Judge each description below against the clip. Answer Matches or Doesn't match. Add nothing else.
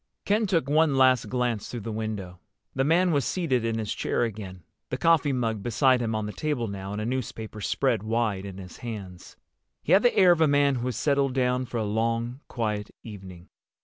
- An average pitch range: Matches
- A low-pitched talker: Matches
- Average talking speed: Doesn't match